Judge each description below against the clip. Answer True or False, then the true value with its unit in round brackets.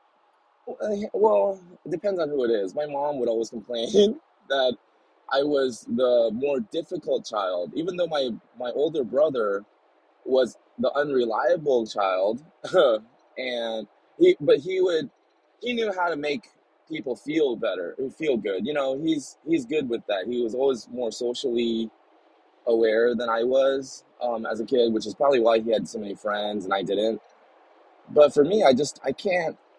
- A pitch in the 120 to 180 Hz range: True (140 Hz)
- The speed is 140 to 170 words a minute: True (165 wpm)